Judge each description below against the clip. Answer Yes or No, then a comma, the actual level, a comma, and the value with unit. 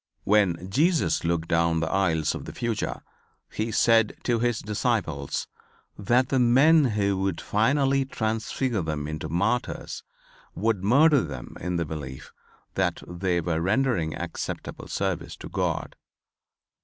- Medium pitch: No, low, 100 Hz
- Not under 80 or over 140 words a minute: Yes, slow, 135 wpm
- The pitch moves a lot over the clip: Yes, wide, 6.4 semitones